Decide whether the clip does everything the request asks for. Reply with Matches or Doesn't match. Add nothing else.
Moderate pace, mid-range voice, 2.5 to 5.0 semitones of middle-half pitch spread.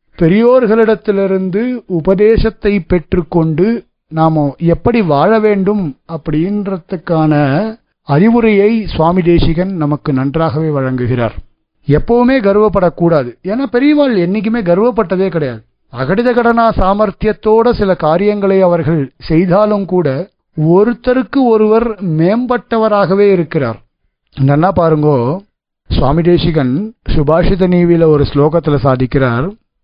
Doesn't match